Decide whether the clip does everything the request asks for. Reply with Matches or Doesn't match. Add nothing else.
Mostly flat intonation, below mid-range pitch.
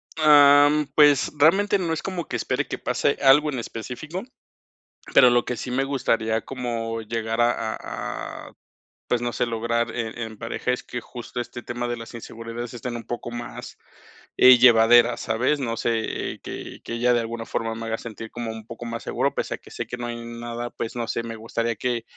Matches